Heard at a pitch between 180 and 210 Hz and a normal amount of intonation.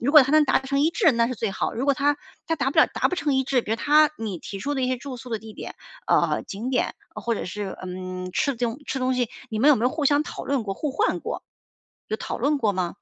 No: very high, 255 Hz; average, 4.6 semitones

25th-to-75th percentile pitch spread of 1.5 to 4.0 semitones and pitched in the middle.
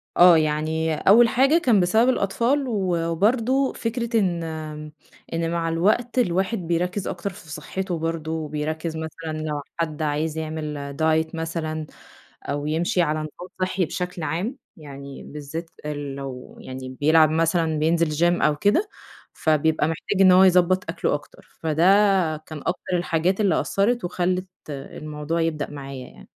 Yes: average, 3.2 semitones; medium, 165 Hz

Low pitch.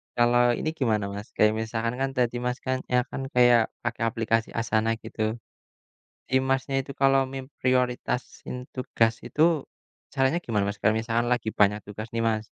Yes: low, 120 Hz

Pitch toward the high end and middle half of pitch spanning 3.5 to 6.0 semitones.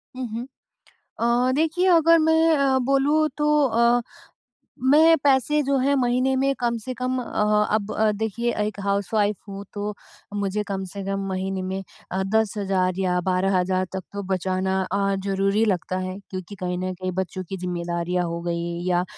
Yes: high, 200 Hz; wide, 5.5 semitones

